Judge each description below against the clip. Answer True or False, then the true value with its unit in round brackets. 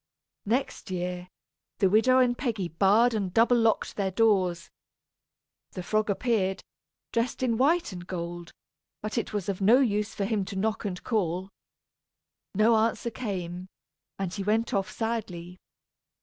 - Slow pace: False (150 wpm)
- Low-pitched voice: False (205 Hz)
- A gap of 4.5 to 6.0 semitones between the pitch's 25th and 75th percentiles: False (3.7 semitones)